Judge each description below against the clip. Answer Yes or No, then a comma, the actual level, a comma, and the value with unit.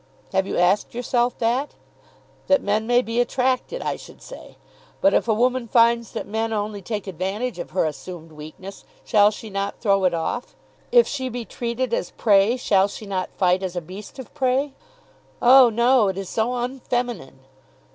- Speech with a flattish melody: No, average, 4.1 semitones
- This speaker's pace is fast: No, average, 180 wpm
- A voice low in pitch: No, high, 225 Hz